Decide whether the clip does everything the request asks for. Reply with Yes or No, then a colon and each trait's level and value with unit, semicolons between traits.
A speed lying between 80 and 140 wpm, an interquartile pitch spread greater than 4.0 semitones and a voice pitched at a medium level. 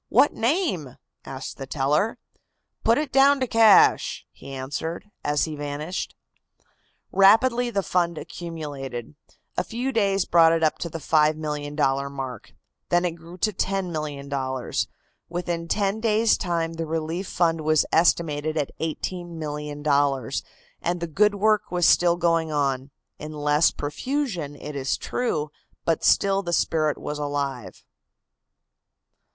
Yes: slow, 135 wpm; average, 4.5 semitones; medium, 165 Hz